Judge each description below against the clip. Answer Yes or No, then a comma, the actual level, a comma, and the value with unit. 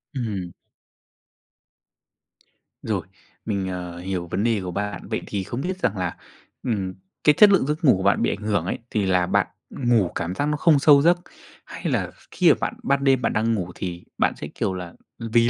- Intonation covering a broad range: Yes, wide, 6.4 semitones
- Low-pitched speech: Yes, low, 105 Hz